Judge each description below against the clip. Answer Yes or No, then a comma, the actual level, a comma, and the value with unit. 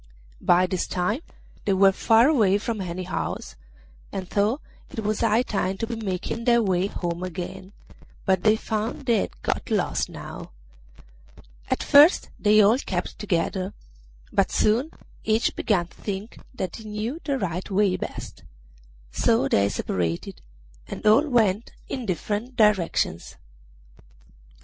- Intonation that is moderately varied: Yes, average, 3.5 semitones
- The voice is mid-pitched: No, high, 210 Hz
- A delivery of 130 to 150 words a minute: Yes, average, 145 wpm